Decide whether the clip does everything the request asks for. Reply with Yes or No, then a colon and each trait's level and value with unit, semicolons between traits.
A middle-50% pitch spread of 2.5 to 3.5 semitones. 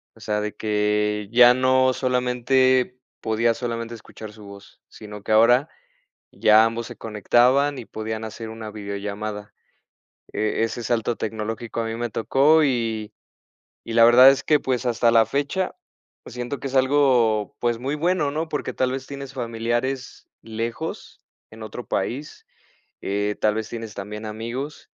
Yes: average, 3.1 semitones